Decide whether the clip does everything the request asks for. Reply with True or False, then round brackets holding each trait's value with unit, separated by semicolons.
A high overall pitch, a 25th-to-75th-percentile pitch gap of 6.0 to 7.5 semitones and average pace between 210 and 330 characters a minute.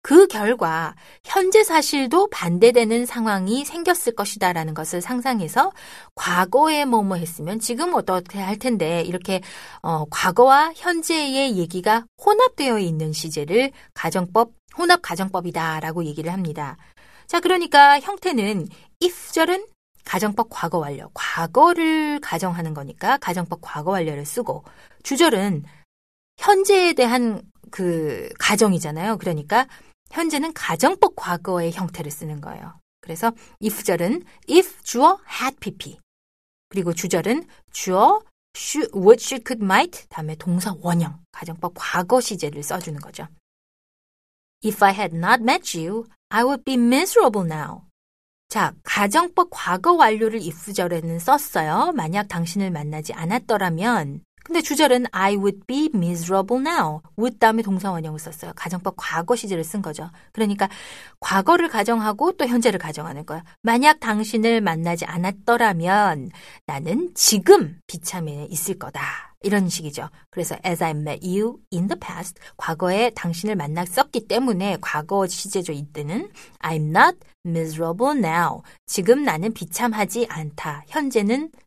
False (205 Hz; 6.9 semitones; 340 characters per minute)